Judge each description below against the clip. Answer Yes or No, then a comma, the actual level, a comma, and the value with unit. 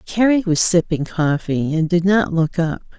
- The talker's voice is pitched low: No, medium, 175 Hz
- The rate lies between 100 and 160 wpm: No, average, 180 wpm